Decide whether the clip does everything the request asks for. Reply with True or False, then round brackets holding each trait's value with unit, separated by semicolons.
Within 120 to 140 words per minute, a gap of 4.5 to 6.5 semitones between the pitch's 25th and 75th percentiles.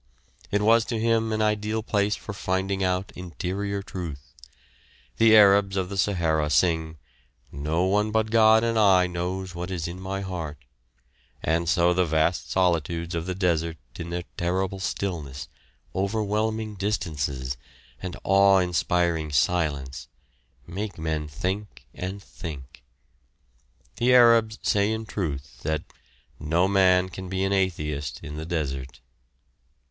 False (135 wpm; 3.9 semitones)